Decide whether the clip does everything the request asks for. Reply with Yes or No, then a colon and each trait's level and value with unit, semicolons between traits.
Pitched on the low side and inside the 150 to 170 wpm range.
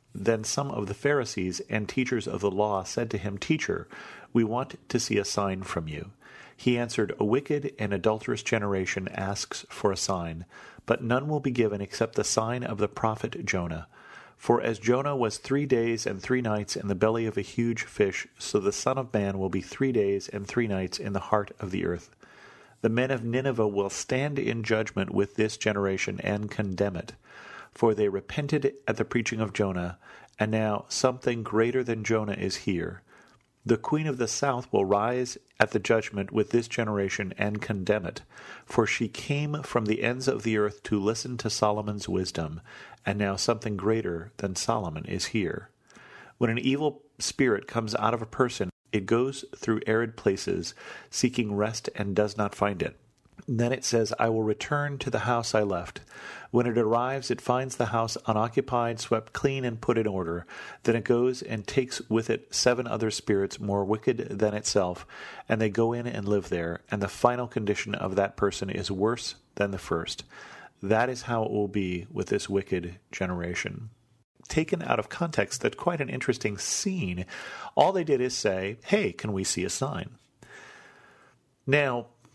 No: low, 110 Hz; average, 185 wpm